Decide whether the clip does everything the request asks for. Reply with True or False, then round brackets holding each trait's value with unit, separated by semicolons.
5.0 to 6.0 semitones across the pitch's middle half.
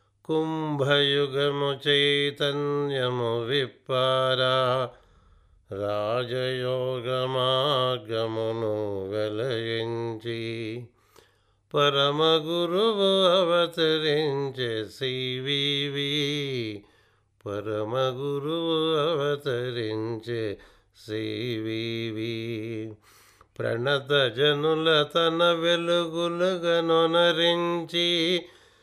True (5.4 semitones)